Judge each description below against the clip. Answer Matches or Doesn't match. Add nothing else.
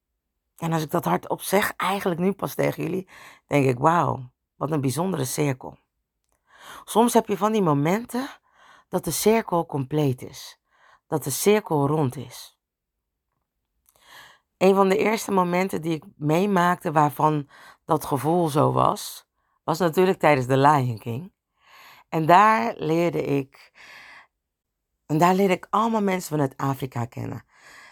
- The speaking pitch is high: Doesn't match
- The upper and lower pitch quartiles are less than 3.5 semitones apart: Doesn't match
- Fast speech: Doesn't match